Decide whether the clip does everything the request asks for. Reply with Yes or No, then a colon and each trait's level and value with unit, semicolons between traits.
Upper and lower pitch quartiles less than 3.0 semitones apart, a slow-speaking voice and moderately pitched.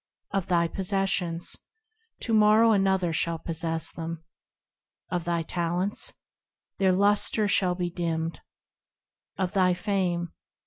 Yes: narrow, 2.6 semitones; slow, 115 wpm; medium, 180 Hz